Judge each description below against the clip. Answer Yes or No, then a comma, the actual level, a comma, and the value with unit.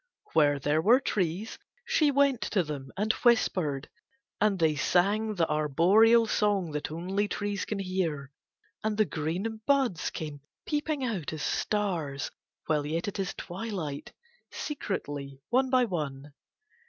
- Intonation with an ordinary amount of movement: No, wide, 6.2 semitones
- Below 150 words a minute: Yes, average, 140 wpm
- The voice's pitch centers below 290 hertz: Yes, medium, 185 Hz